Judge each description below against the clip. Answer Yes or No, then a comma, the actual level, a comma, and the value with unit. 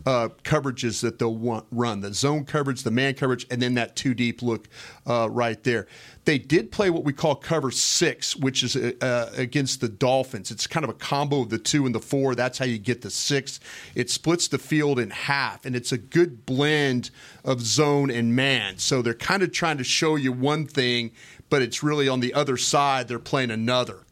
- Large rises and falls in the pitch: No, average, 3.0 semitones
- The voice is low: Yes, low, 130 Hz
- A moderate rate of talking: No, fast, 215 wpm